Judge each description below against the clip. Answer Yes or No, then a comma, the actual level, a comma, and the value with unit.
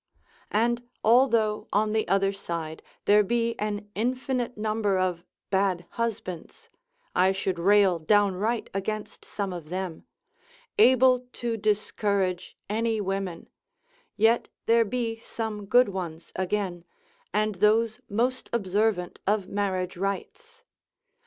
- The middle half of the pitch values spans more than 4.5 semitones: No, average, 3.1 semitones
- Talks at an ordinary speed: No, slow, 115 wpm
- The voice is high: Yes, high, 210 Hz